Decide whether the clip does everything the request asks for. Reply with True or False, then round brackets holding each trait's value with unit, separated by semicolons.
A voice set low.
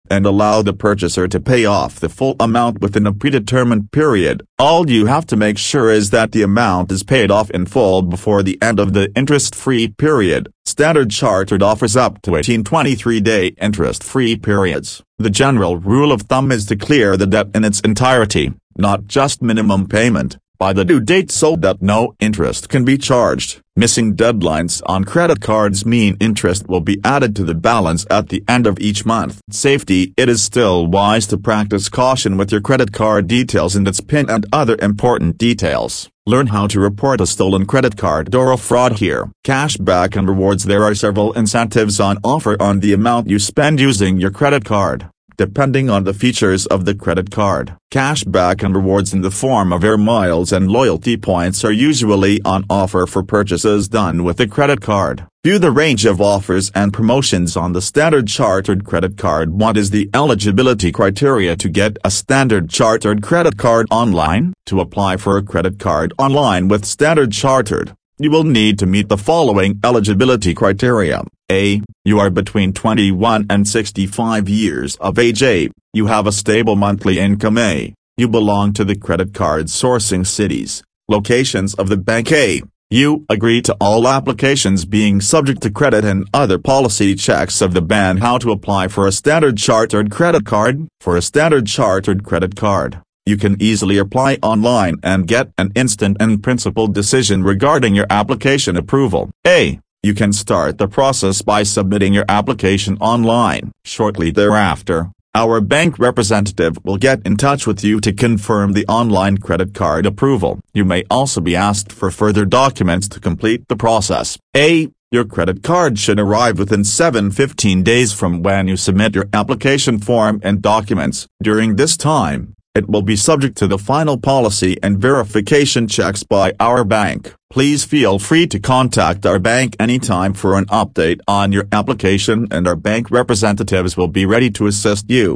True (105 Hz)